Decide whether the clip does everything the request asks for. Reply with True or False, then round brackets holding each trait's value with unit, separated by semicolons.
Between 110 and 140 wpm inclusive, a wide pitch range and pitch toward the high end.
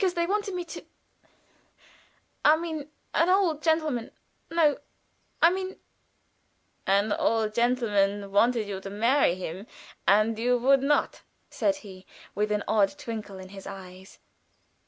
True (135 wpm; 7.3 semitones; 230 Hz)